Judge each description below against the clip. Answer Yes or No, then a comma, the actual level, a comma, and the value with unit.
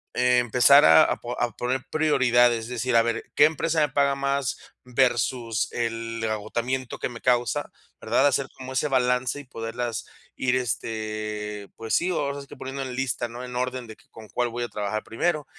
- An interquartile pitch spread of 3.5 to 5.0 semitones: No, narrow, 2.6 semitones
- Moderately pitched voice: No, low, 125 Hz